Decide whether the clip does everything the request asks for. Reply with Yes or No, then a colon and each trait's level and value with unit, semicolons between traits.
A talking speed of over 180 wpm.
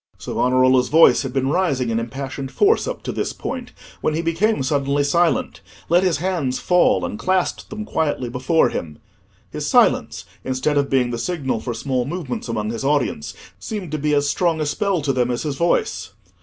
Yes: average, 195 wpm